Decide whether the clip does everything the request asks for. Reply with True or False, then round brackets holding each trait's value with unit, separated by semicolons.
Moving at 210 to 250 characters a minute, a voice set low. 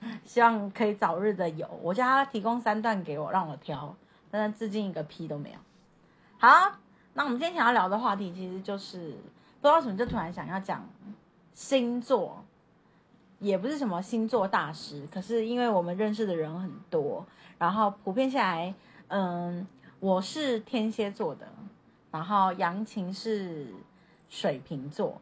False (240 characters per minute; 200 Hz)